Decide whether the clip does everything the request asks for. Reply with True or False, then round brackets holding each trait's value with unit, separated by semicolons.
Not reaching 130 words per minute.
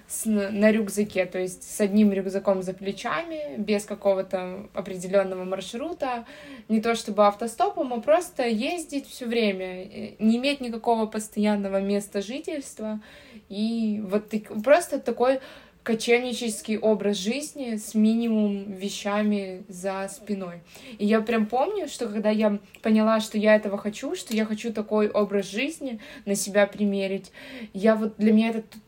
False (145 wpm)